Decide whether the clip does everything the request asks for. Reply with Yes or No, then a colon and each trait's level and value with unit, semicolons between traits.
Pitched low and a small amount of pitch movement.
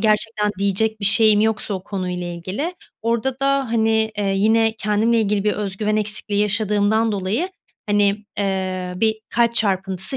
No: high, 210 Hz; narrow, 2.1 semitones